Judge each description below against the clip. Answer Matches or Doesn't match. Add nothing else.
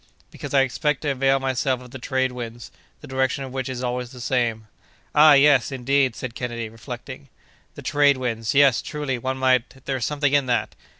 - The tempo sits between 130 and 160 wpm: Doesn't match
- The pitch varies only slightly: Matches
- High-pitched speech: Doesn't match